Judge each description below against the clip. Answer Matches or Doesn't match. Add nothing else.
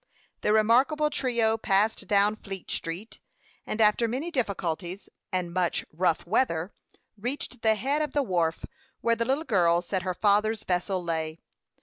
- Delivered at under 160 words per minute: Matches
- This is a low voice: Doesn't match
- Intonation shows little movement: Doesn't match